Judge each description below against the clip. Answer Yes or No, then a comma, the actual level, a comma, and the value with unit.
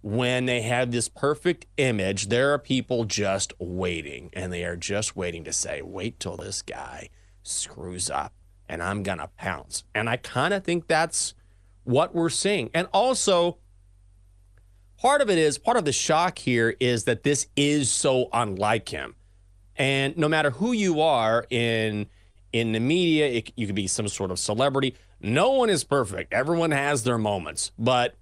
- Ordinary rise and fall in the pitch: No, wide, 6.8 semitones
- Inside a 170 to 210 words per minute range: Yes, average, 175 wpm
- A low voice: Yes, low, 115 Hz